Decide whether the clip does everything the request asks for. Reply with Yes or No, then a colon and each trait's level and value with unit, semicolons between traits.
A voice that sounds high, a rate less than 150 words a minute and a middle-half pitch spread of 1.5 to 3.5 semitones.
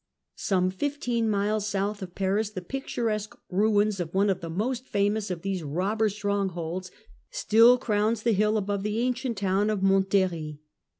No: high, 205 Hz; average, 160 wpm; narrow, 2.4 semitones